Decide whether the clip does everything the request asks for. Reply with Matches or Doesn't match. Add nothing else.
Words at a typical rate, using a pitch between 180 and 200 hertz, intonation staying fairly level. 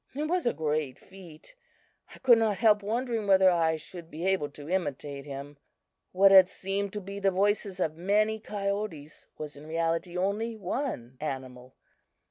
Doesn't match